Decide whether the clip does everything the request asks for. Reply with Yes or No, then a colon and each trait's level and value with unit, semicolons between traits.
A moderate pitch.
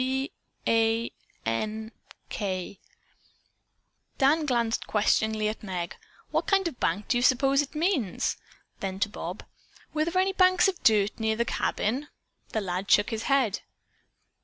No: high, 225 Hz